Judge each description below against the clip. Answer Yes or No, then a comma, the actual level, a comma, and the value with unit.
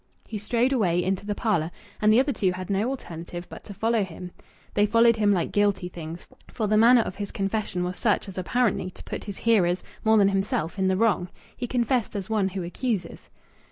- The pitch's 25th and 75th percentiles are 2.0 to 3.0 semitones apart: No, average, 3.6 semitones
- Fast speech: Yes, fast, 215 wpm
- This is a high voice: Yes, high, 200 Hz